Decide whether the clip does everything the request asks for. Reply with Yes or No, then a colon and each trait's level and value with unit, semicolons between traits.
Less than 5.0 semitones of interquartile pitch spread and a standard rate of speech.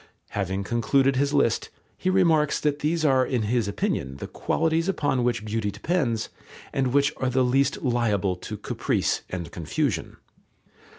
No: wide, 5.4 semitones; average, 155 wpm